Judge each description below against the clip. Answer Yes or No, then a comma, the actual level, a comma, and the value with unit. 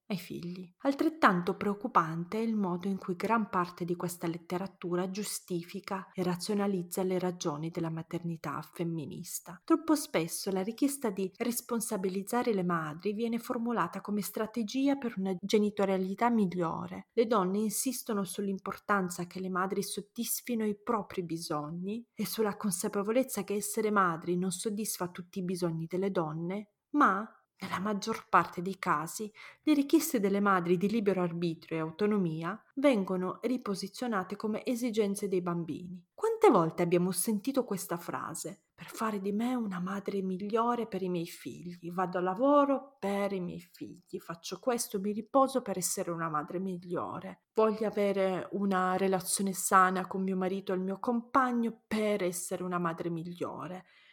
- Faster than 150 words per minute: No, average, 145 wpm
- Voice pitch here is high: Yes, high, 195 Hz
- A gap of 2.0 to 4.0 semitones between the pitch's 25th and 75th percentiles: Yes, average, 3.6 semitones